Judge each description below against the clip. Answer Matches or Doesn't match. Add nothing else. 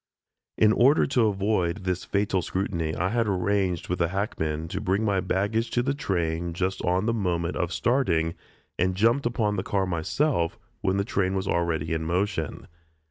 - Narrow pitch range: Doesn't match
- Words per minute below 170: Doesn't match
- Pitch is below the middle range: Matches